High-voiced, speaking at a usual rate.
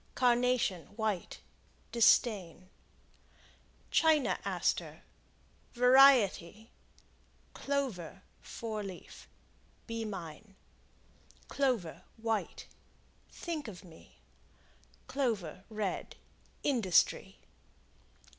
No: high, 220 Hz; slow, 60 wpm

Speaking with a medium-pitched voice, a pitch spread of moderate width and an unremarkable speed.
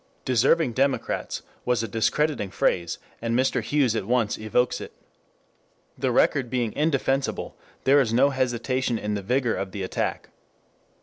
No: low, 125 Hz; average, 3.4 semitones; average, 145 wpm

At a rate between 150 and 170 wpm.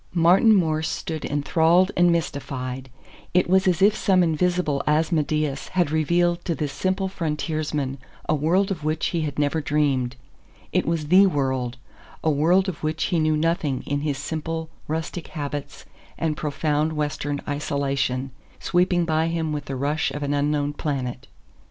Yes: average, 160 wpm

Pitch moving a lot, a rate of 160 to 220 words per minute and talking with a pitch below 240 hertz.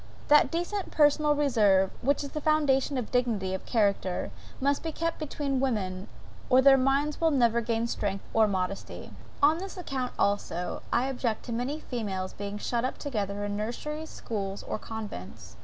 No: wide, 6.0 semitones; average, 175 wpm; high, 245 Hz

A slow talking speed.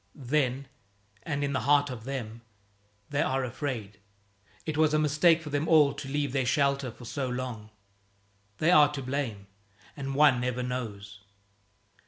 No: average, 160 wpm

